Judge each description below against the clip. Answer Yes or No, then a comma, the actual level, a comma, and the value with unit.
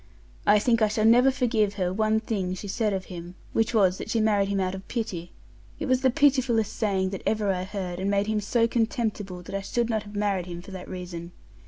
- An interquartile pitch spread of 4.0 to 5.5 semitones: No, average, 3.0 semitones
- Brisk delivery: Yes, fast, 235 wpm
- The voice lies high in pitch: Yes, high, 205 Hz